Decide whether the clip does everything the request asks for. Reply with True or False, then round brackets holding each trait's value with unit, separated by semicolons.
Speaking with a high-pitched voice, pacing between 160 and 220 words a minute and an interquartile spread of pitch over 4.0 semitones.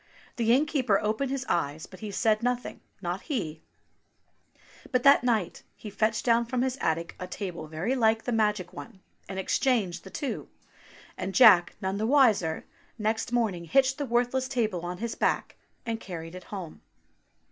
True (220 Hz; 175 wpm; 5.1 semitones)